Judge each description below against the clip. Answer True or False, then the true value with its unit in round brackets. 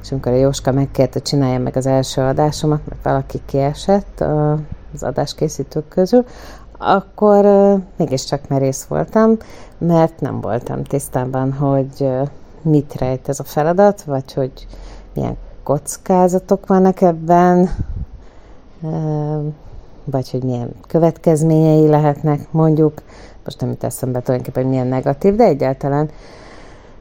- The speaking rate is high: False (120 wpm)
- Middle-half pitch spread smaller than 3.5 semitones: False (3.8 semitones)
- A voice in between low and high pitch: True (145 Hz)